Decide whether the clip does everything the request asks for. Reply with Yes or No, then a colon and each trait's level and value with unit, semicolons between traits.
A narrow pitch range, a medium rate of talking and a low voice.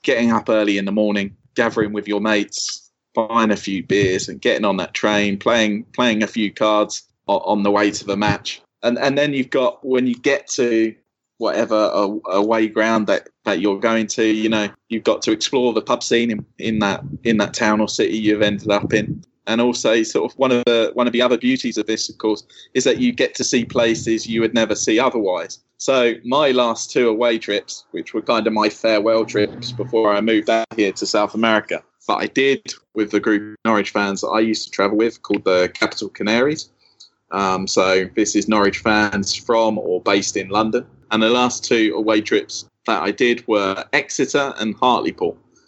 No: narrow, 1.9 semitones; fast, 210 wpm; low, 110 Hz